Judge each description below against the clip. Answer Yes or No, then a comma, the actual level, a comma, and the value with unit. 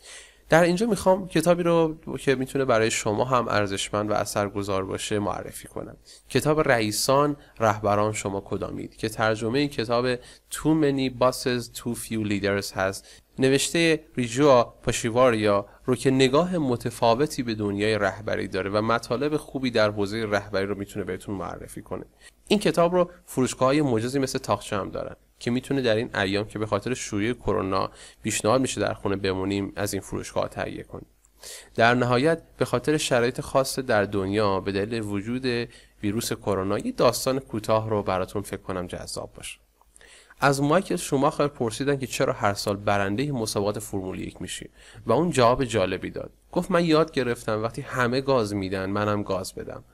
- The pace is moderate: No, fast, 165 wpm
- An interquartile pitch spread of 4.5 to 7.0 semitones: Yes, average, 5.0 semitones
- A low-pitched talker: Yes, low, 115 Hz